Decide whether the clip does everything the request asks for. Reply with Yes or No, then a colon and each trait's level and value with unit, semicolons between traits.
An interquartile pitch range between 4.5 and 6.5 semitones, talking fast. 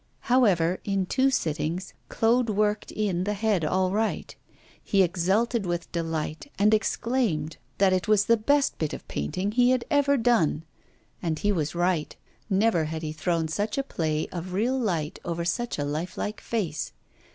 No: average, 5.3 semitones; average, 170 wpm